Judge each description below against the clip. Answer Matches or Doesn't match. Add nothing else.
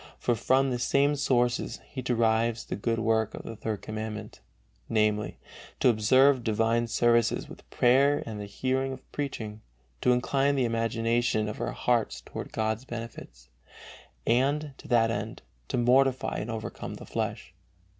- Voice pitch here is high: Doesn't match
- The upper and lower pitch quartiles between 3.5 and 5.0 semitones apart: Doesn't match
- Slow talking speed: Doesn't match